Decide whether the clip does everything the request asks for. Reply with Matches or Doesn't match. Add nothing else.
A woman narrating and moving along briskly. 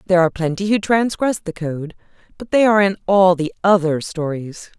Doesn't match